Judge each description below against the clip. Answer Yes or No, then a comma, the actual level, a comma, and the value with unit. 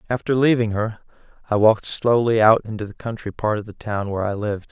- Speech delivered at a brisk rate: Yes, fast, 215 wpm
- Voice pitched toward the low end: Yes, low, 110 Hz